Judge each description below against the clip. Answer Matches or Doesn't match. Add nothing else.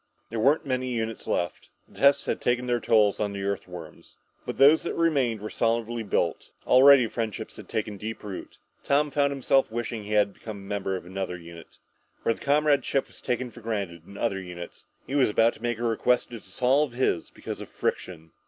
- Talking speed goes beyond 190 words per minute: Matches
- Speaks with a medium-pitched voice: Doesn't match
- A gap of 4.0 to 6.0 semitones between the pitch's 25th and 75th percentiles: Matches